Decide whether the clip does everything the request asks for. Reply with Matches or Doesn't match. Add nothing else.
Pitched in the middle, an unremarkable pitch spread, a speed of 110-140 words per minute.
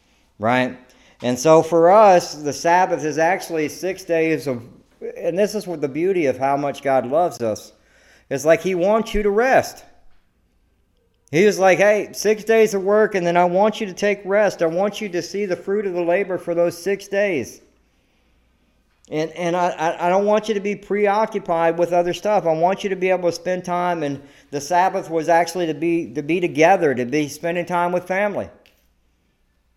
Doesn't match